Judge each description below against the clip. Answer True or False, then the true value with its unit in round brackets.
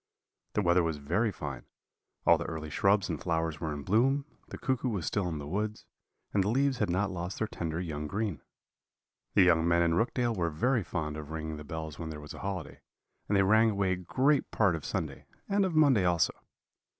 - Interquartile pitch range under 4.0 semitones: False (5.1 semitones)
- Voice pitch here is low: True (90 Hz)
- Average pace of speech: False (210 wpm)